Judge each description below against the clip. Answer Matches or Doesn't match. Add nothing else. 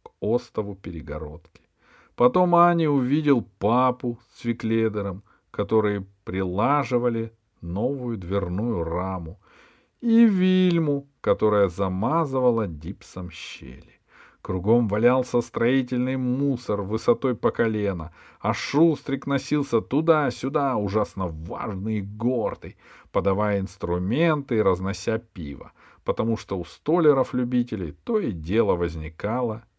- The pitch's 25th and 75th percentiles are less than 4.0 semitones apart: Doesn't match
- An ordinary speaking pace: Doesn't match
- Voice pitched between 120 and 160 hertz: Doesn't match